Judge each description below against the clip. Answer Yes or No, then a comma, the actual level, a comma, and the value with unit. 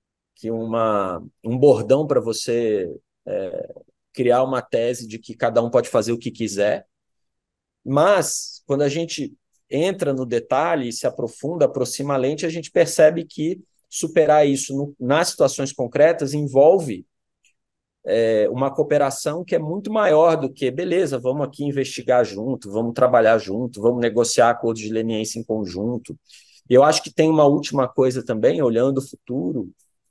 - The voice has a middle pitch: No, low, 130 Hz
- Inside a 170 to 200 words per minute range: No, average, 155 wpm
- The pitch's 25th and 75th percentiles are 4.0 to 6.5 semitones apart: Yes, average, 4.4 semitones